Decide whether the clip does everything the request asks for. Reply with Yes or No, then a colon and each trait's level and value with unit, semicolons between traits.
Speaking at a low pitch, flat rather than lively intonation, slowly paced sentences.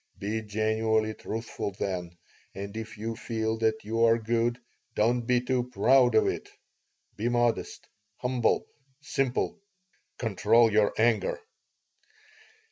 Yes: low, 115 Hz; narrow, 1.8 semitones; slow, 120 wpm